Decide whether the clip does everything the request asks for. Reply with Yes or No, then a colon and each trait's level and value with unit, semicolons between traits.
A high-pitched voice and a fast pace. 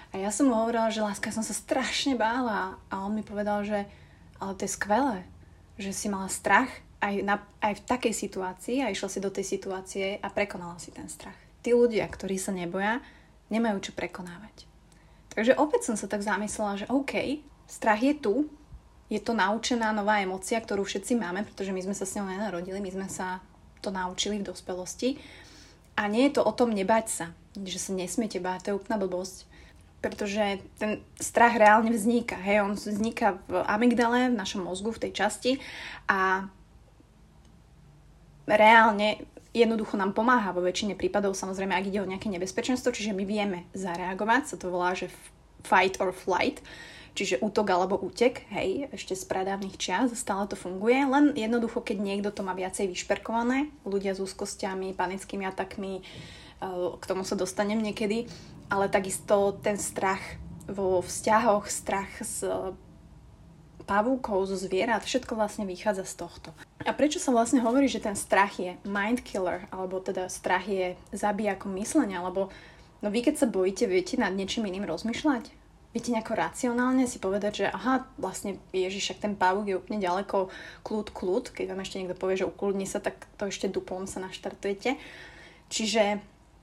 Yes: high, 205 Hz; fast, 170 wpm